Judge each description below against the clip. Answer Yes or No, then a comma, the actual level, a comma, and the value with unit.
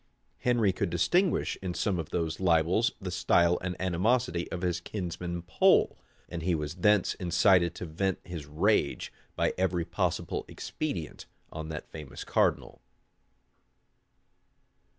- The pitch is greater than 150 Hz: No, very low, 90 Hz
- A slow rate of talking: Yes, slow, 130 wpm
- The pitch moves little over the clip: Yes, narrow, 2.3 semitones